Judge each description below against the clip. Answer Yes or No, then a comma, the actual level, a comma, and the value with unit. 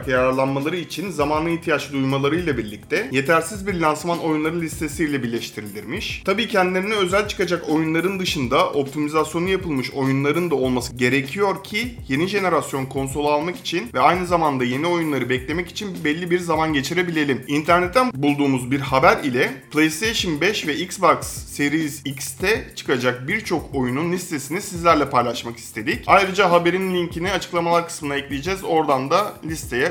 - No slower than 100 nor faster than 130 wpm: No, fast, 140 wpm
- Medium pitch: Yes, medium, 155 Hz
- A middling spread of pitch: Yes, average, 4.3 semitones